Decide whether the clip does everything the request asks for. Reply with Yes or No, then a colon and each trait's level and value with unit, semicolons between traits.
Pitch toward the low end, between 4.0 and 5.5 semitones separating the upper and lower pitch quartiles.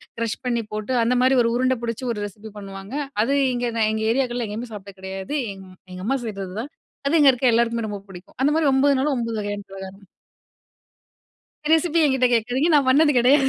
No: high, 235 Hz; average, 4.4 semitones